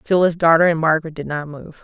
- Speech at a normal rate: No, fast, 260 wpm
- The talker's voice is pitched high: No, medium, 160 Hz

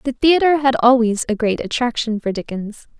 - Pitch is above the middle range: Yes, high, 240 Hz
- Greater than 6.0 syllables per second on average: No, 5.1 syllables/s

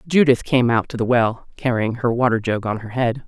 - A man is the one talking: No, female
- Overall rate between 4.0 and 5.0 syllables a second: No, 5.3 syllables/s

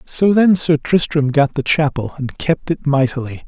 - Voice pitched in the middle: Yes, medium, 145 Hz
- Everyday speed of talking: Yes, average, 190 wpm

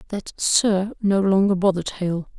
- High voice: Yes, high, 195 Hz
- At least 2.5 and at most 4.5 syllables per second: Yes, 4.4 syllables/s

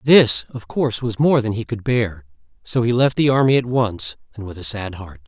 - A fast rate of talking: Yes, fast, 250 wpm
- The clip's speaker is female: No, male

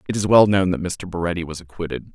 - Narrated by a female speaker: No, male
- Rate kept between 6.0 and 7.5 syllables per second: Yes, 6.5 syllables/s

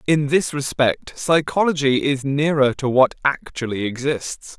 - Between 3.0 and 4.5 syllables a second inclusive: Yes, 4.2 syllables/s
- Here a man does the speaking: Yes, male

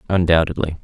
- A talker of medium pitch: No, very low, 85 Hz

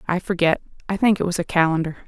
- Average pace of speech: No, fast, 230 wpm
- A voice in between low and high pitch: Yes, medium, 175 Hz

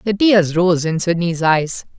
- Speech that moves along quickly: No, average, 180 wpm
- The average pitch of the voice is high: No, medium, 175 Hz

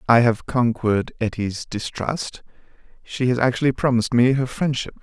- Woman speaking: No, male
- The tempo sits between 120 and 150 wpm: Yes, average, 145 wpm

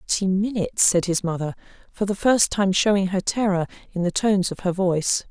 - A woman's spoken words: Yes, female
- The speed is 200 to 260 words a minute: Yes, fast, 205 wpm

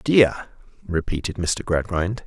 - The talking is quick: No, slow, 105 wpm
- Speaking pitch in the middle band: No, very low, 90 Hz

